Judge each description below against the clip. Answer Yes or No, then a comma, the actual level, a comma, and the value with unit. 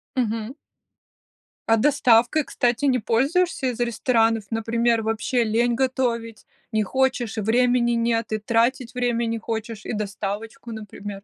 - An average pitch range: No, narrow, 2.0 semitones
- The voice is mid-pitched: No, high, 230 Hz